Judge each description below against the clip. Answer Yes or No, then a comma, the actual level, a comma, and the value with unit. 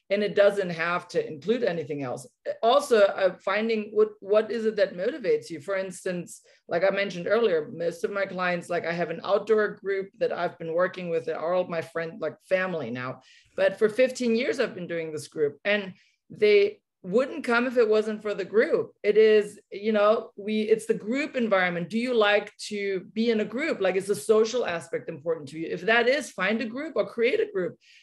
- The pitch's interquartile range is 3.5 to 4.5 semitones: Yes, average, 4.0 semitones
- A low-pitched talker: No, high, 205 Hz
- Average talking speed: No, fast, 215 wpm